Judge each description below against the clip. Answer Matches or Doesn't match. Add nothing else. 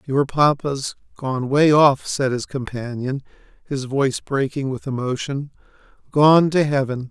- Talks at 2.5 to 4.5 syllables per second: Matches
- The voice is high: Doesn't match